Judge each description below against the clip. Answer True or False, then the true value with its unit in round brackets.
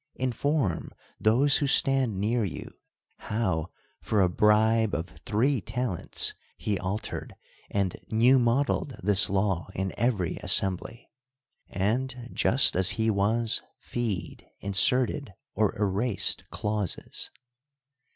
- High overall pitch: False (110 Hz)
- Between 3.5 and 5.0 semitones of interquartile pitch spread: True (4.1 semitones)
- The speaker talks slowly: True (110 wpm)